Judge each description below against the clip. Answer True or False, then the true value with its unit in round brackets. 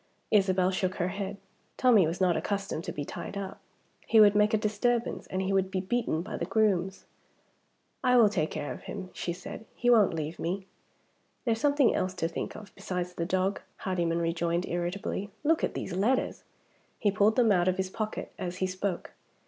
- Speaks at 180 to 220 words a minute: True (195 wpm)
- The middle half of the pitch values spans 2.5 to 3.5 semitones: True (3.1 semitones)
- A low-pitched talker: False (190 Hz)